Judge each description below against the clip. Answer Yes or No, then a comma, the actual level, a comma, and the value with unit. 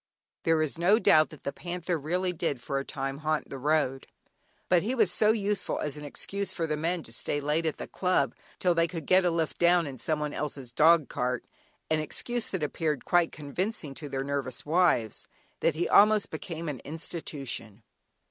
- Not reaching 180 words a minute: No, average, 195 wpm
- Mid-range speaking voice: Yes, medium, 155 Hz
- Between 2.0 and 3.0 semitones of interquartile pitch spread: No, average, 3.9 semitones